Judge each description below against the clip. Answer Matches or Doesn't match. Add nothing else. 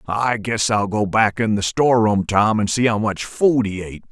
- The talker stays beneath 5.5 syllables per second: Matches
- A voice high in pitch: Doesn't match